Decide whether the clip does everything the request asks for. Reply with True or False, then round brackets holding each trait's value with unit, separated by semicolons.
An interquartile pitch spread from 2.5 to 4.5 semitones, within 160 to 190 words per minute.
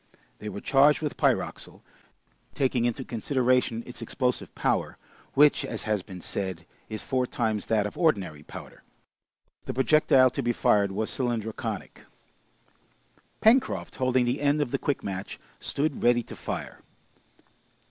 False (4.0 semitones; 140 wpm)